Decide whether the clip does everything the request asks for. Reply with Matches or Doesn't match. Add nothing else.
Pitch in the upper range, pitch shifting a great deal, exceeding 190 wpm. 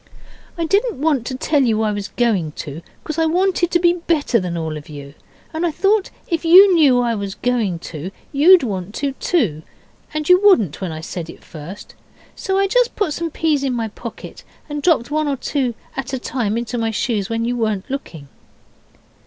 Matches